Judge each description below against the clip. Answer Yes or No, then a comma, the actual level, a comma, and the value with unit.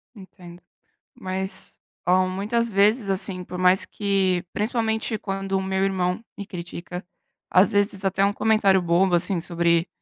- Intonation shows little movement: Yes, narrow, 1.9 semitones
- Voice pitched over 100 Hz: Yes, high, 190 Hz